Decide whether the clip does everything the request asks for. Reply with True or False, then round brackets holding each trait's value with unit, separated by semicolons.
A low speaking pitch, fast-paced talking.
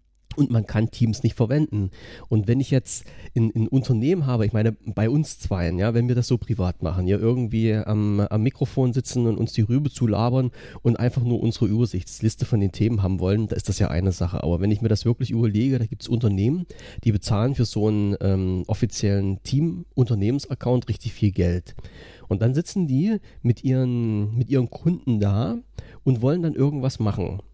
True (115 Hz; 195 wpm)